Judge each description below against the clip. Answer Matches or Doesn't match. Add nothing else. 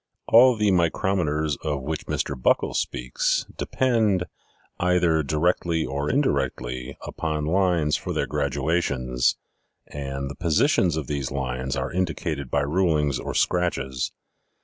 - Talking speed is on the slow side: Matches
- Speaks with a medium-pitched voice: Doesn't match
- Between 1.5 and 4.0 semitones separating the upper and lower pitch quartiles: Doesn't match